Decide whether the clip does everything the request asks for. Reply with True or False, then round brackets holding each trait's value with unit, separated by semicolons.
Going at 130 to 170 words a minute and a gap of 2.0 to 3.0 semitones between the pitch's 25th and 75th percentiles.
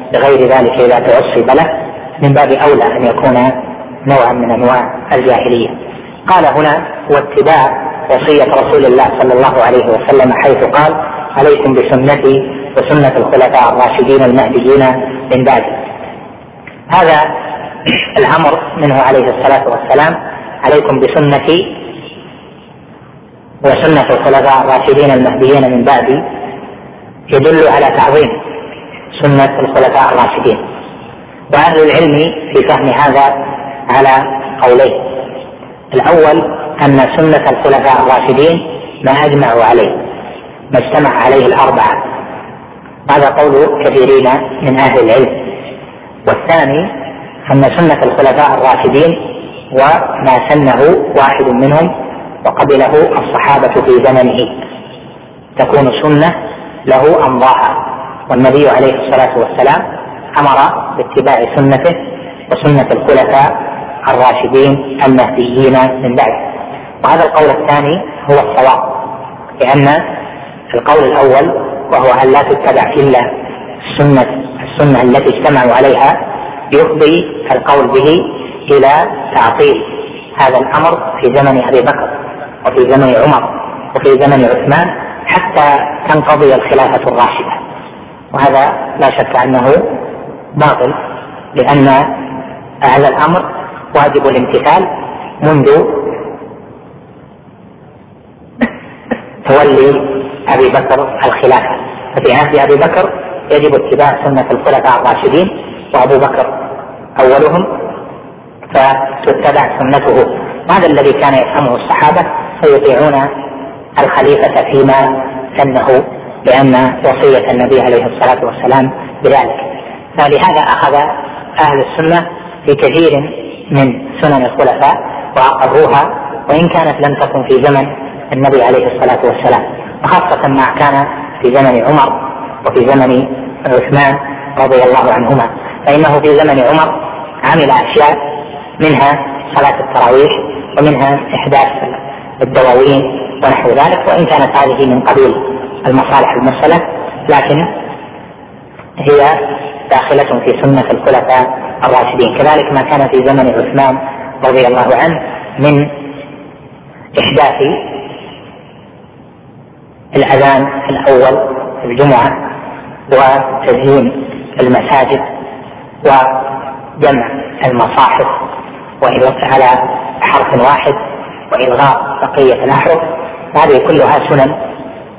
False (95 wpm; 2.7 semitones)